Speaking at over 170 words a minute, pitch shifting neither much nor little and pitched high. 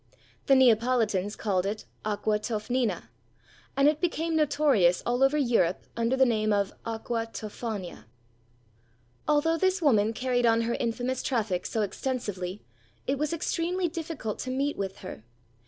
No: average, 140 wpm; average, 5.0 semitones; high, 235 Hz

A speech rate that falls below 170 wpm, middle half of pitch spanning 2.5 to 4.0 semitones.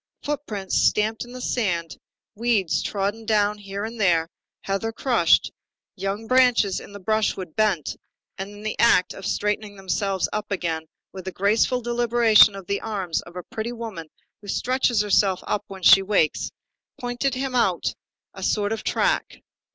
Yes: average, 160 wpm; average, 2.9 semitones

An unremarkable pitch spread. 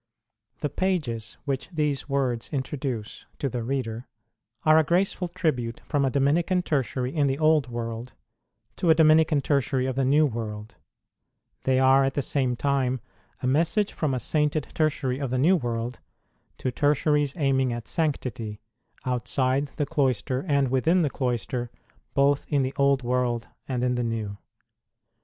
Yes: average, 3.1 semitones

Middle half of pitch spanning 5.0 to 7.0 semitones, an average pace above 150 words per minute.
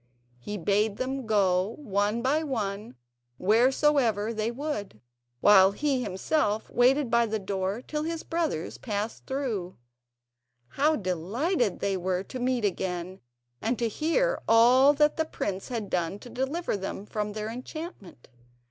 No: average, 5.3 semitones; average, 140 wpm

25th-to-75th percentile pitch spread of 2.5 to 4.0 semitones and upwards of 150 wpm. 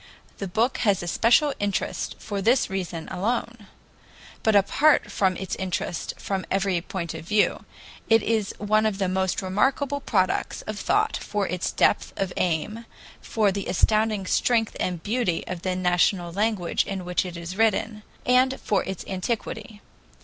Yes: average, 3.3 semitones; average, 160 wpm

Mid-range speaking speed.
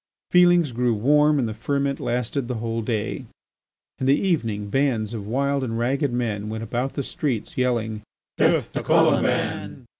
Yes: average, 160 wpm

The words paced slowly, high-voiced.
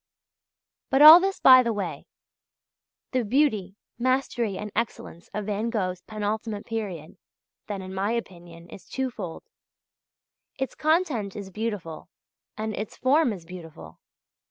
Yes: slow, 130 wpm; high, 210 Hz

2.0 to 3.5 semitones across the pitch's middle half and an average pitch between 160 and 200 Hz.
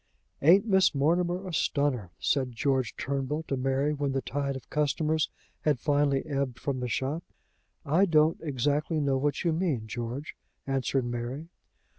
No: average, 2.9 semitones; medium, 140 Hz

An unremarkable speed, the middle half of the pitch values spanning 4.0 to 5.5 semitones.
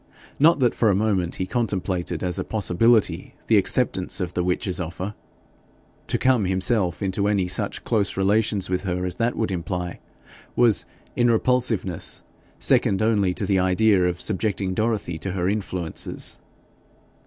No: average, 155 wpm; average, 3.4 semitones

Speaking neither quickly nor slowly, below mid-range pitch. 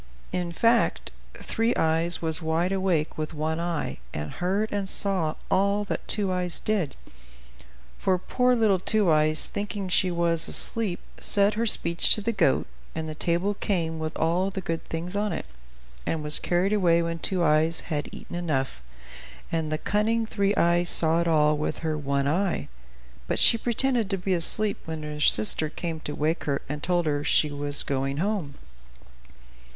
No: average, 175 wpm; medium, 170 Hz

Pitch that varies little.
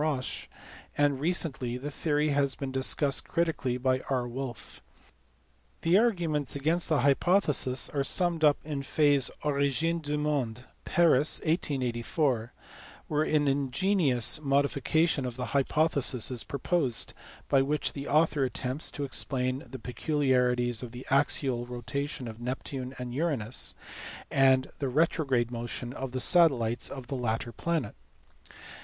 No: average, 3.2 semitones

